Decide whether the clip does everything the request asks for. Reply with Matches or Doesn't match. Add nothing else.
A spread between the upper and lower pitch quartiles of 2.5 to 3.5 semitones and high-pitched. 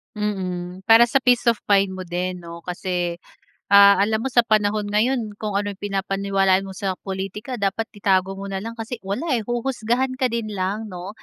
Matches